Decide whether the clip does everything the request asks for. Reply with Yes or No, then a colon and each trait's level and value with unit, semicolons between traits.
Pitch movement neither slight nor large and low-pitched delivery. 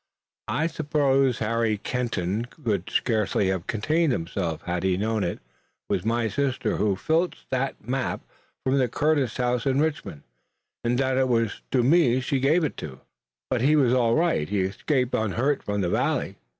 Yes: average, 4.6 semitones; low, 125 Hz